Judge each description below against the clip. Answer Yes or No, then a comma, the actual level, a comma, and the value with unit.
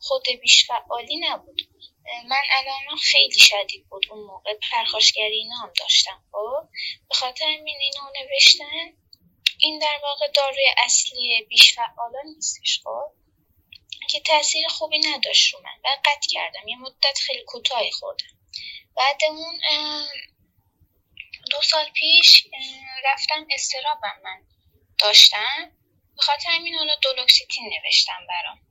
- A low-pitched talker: No, very high, 285 Hz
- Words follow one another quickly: No, average, 115 wpm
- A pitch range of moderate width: Yes, average, 3.4 semitones